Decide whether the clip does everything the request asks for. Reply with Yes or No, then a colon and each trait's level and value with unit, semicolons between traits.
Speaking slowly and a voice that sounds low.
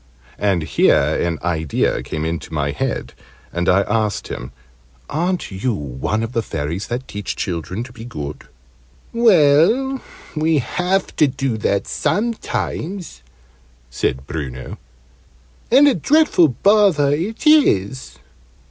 Yes: slow, 125 wpm; low, 120 Hz